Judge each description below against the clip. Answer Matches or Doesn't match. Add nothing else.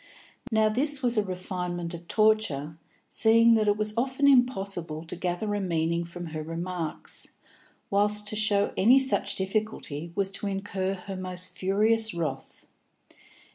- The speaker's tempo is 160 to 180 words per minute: Doesn't match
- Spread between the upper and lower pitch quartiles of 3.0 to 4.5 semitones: Matches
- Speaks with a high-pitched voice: Matches